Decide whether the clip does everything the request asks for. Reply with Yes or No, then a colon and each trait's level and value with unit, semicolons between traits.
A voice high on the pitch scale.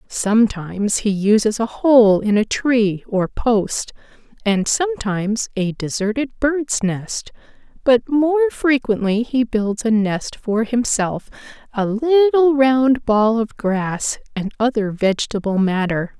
Yes: high, 225 Hz